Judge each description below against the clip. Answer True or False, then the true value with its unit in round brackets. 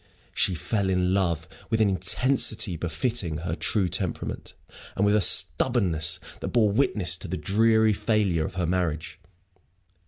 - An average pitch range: True (4.2 semitones)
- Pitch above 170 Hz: False (95 Hz)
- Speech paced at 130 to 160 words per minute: True (150 wpm)